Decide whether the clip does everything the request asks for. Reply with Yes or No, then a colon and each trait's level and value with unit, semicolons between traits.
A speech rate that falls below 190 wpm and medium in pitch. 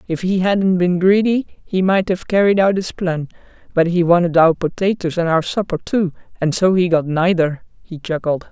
No: average, 195 wpm; medium, 180 Hz